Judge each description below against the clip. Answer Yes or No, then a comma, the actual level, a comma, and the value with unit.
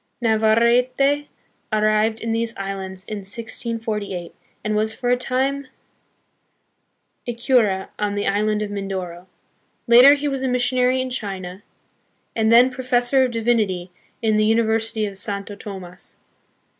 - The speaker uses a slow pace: Yes, slow, 130 wpm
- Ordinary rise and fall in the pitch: Yes, average, 3.5 semitones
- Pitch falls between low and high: No, high, 220 Hz